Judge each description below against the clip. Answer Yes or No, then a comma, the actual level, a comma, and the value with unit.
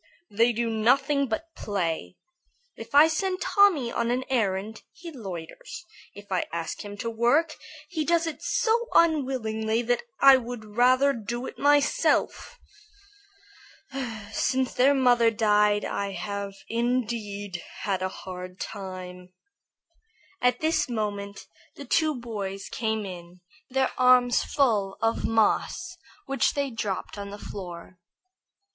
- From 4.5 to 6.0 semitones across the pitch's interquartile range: Yes, average, 5.0 semitones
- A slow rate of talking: Yes, slow, 130 wpm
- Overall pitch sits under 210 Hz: No, high, 230 Hz